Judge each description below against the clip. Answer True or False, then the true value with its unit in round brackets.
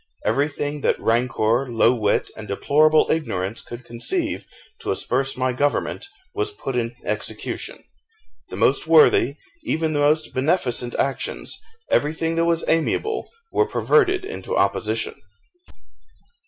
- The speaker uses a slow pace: True (125 wpm)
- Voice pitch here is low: False (145 Hz)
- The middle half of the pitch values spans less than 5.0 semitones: False (5.4 semitones)